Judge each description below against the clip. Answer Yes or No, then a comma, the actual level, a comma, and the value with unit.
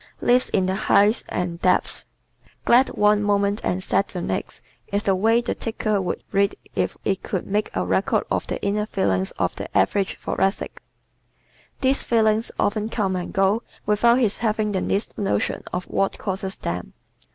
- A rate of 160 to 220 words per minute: Yes, average, 175 wpm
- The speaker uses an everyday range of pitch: No, narrow, 2.2 semitones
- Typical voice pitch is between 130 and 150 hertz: No, high, 200 Hz